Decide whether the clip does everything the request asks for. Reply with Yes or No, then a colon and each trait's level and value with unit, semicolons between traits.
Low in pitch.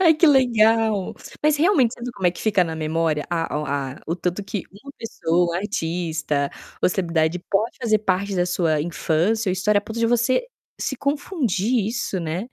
No: high, 195 Hz